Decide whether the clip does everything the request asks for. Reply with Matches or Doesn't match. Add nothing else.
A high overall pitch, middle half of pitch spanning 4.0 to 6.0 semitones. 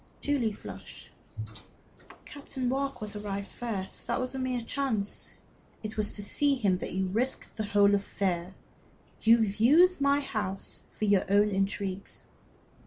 Matches